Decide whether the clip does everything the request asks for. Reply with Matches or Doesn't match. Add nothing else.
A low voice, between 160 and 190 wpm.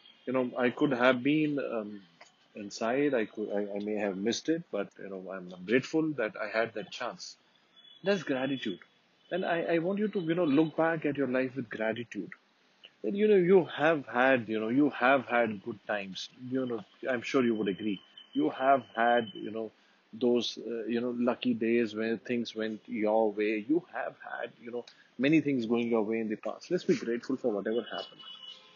Doesn't match